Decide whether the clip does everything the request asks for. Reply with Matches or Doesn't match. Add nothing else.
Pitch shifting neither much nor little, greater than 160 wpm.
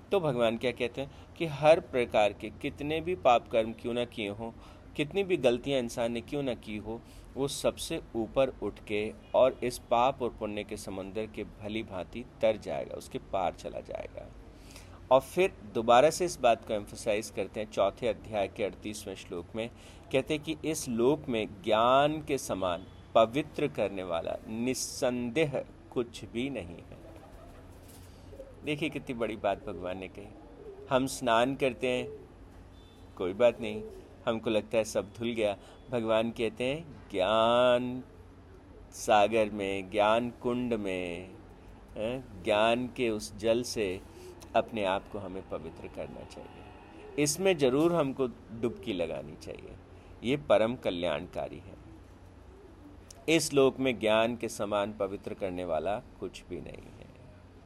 Doesn't match